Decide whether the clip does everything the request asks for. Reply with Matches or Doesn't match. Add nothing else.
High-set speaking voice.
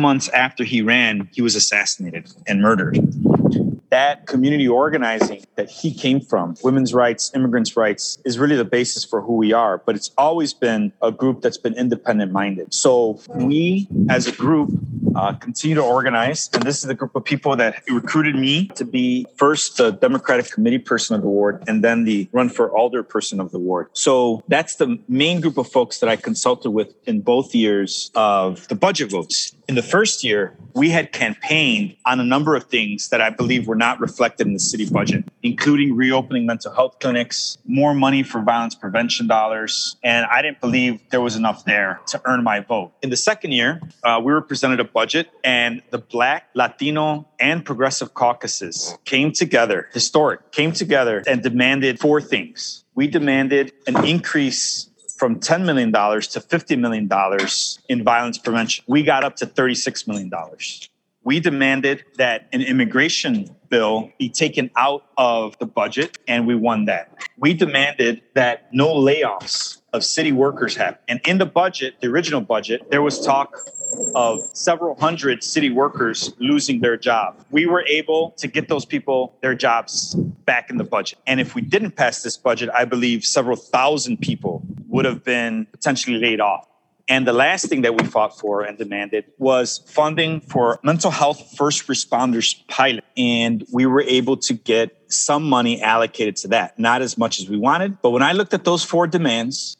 Doesn't match